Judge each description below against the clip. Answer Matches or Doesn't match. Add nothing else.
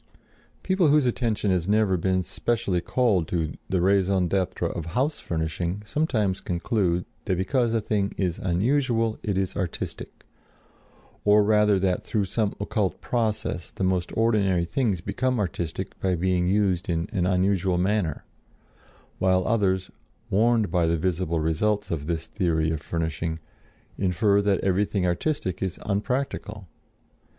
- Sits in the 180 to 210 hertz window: Doesn't match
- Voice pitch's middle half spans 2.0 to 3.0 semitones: Doesn't match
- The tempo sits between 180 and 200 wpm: Doesn't match